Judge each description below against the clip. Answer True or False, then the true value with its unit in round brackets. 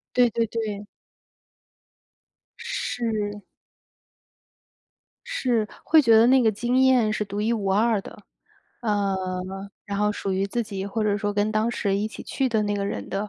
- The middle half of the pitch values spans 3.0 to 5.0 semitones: False (2.5 semitones)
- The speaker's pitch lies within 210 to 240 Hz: True (215 Hz)